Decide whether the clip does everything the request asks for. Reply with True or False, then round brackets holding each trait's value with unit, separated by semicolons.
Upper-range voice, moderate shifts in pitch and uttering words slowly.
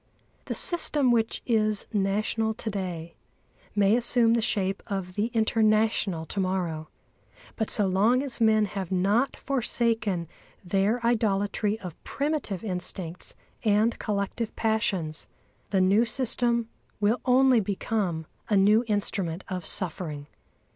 True (210 Hz; 3.4 semitones; 125 wpm)